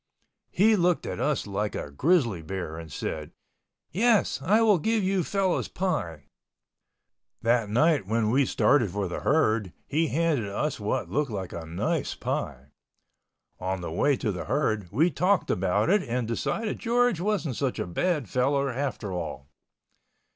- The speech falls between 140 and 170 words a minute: Yes, average, 160 wpm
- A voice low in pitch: Yes, low, 125 Hz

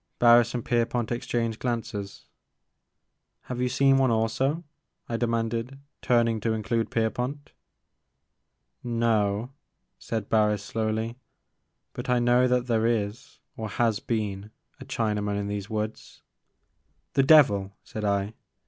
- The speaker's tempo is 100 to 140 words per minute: Yes, slow, 135 wpm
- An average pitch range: No, narrow, 2.2 semitones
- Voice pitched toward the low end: Yes, low, 115 Hz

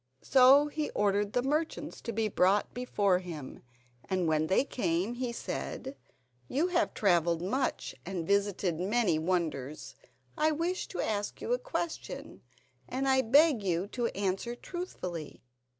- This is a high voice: Yes, high, 210 Hz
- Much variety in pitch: Yes, wide, 7.0 semitones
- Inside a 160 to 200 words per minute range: No, average, 145 wpm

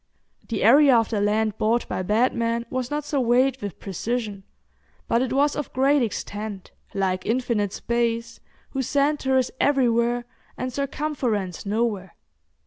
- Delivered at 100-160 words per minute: Yes, slow, 135 wpm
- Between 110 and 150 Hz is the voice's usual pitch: No, high, 235 Hz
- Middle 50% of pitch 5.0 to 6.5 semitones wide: No, average, 3.8 semitones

